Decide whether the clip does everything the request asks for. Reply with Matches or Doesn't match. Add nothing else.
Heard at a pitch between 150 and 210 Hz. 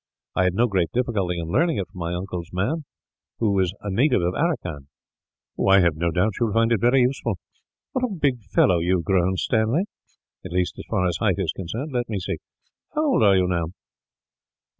Doesn't match